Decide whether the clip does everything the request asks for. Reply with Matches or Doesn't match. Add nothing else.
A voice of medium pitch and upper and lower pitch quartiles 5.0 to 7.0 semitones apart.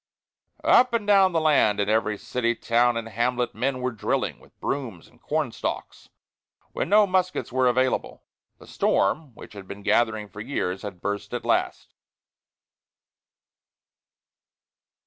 Doesn't match